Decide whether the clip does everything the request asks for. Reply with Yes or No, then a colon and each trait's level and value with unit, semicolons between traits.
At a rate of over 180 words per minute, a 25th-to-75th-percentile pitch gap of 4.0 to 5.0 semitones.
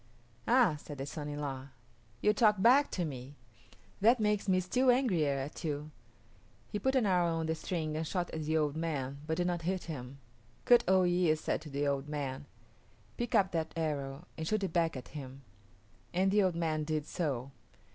Yes: average, 200 wpm; average, 4.5 semitones